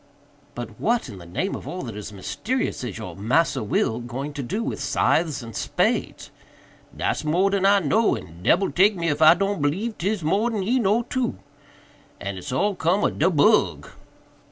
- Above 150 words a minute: Yes, average, 195 wpm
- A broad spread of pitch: Yes, wide, 8.9 semitones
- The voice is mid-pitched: Yes, medium, 165 Hz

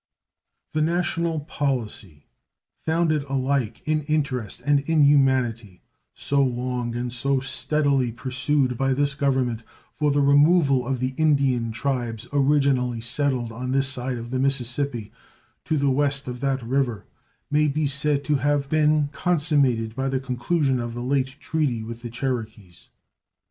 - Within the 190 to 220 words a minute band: No, average, 145 wpm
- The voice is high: No, low, 135 Hz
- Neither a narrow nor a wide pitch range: Yes, average, 3.0 semitones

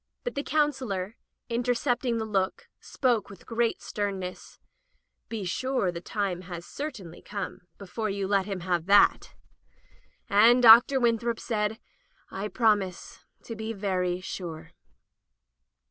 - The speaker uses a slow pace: Yes, slow, 130 wpm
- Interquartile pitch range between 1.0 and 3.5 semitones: No, average, 3.9 semitones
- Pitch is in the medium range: No, high, 210 Hz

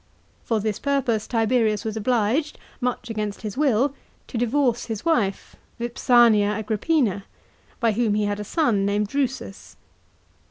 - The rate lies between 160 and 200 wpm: No, average, 145 wpm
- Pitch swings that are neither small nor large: Yes, average, 3.1 semitones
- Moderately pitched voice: No, high, 225 Hz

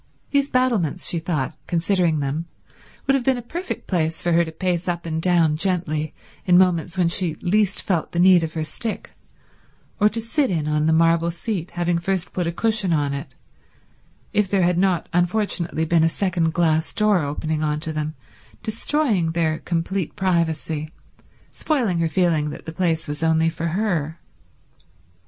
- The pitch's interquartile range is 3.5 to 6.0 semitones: No, average, 2.9 semitones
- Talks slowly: No, average, 175 wpm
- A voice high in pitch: No, medium, 170 Hz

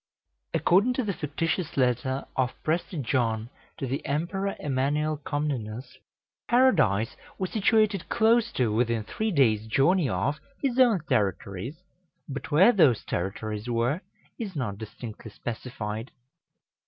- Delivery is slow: Yes, slow, 125 wpm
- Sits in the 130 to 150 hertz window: Yes, medium, 140 Hz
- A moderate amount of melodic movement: No, wide, 8.2 semitones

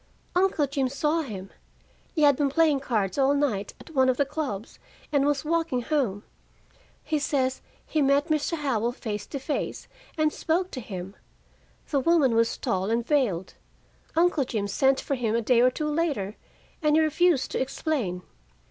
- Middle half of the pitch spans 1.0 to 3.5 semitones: No, average, 4.8 semitones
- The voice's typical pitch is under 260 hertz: No, very high, 275 Hz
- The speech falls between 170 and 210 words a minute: Yes, average, 175 wpm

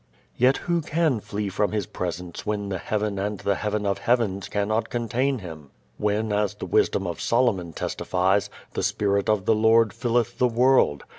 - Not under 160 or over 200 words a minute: Yes, average, 175 wpm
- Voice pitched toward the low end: Yes, low, 105 Hz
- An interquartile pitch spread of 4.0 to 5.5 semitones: No, average, 2.9 semitones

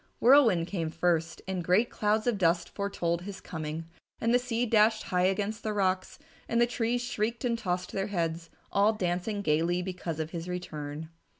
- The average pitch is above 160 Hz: Yes, medium, 185 Hz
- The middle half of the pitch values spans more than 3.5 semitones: Yes, average, 4.3 semitones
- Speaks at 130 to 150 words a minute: No, average, 180 wpm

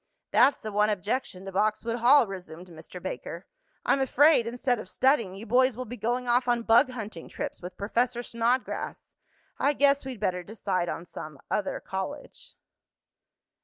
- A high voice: Yes, high, 230 Hz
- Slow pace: No, average, 165 wpm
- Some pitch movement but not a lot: Yes, average, 4.5 semitones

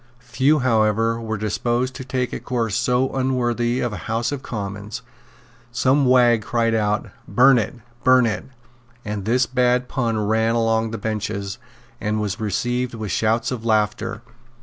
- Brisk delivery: No, average, 155 wpm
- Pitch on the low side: Yes, low, 115 Hz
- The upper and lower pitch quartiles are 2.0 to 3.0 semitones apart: Yes, narrow, 2.5 semitones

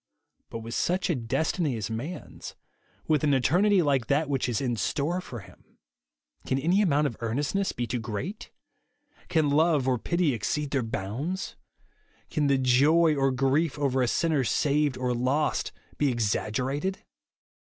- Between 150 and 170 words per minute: Yes, average, 160 wpm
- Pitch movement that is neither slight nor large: Yes, average, 4.3 semitones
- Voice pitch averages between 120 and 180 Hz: Yes, medium, 140 Hz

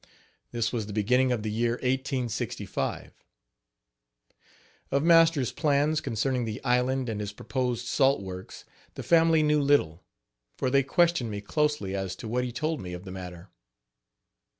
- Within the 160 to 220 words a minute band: No, average, 150 wpm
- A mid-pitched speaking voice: No, low, 125 Hz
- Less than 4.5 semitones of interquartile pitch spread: No, average, 4.9 semitones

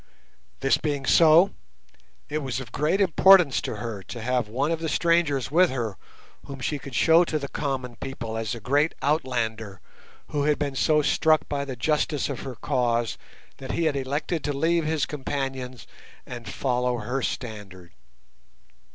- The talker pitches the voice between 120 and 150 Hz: Yes, low, 135 Hz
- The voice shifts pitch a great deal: No, average, 3.9 semitones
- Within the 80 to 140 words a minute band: No, average, 170 wpm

